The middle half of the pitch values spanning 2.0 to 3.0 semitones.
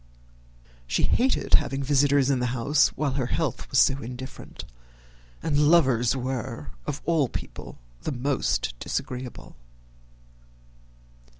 Yes: narrow, 2.5 semitones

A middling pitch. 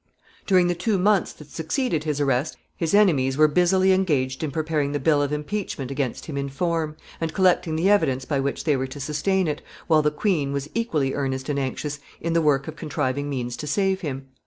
Yes: medium, 150 Hz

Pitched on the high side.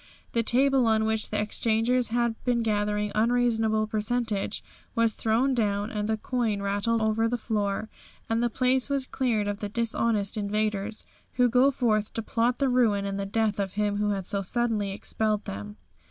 Yes: high, 220 Hz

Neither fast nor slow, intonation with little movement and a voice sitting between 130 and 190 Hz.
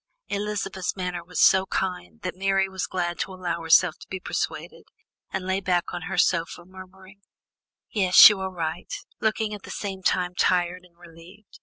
Yes: average, 175 wpm; narrow, 1.5 semitones; medium, 185 Hz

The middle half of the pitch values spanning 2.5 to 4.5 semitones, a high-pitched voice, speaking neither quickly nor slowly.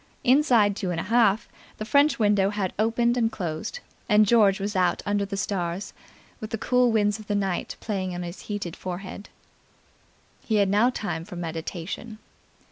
Yes: average, 3.0 semitones; high, 205 Hz; average, 170 wpm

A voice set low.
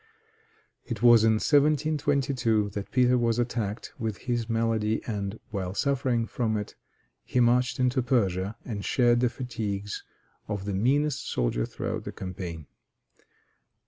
Yes: low, 115 Hz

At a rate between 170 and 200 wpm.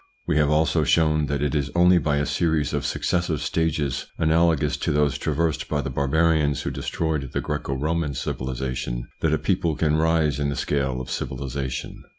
Yes: average, 180 wpm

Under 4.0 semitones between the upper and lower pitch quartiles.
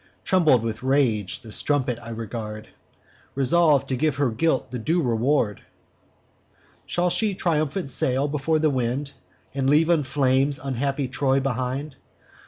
Yes: average, 3.4 semitones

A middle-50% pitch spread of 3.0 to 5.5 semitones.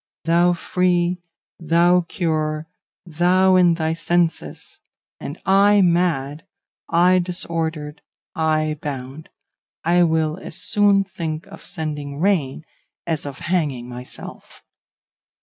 No: narrow, 2.5 semitones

